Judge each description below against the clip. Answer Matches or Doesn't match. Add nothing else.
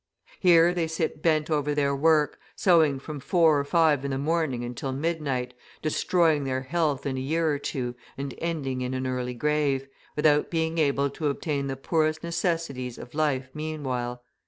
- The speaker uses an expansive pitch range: Doesn't match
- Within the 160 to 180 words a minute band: Matches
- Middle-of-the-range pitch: Matches